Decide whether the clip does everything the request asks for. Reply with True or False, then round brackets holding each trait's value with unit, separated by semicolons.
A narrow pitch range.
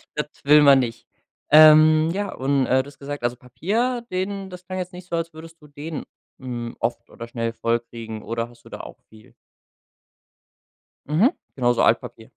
False (5.8 semitones)